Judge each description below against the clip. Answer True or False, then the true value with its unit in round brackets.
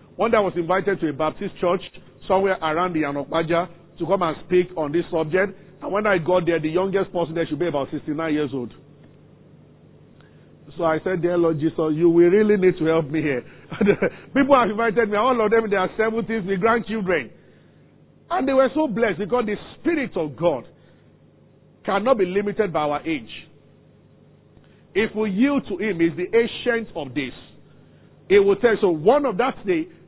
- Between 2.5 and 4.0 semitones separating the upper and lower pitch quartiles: False (5.1 semitones)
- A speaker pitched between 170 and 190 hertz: True (185 Hz)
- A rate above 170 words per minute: True (190 wpm)